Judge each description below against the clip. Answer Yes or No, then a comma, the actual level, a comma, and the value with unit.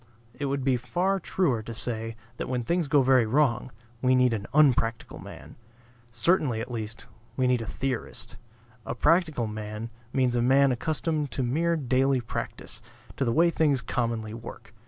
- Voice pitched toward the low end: Yes, low, 130 Hz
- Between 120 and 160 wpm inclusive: No, average, 170 wpm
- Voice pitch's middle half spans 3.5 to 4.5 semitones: Yes, average, 3.9 semitones